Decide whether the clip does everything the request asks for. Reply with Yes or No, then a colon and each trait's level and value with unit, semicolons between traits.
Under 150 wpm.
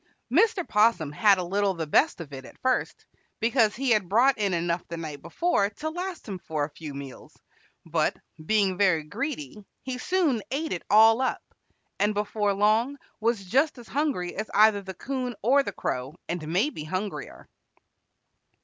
No: average, 175 wpm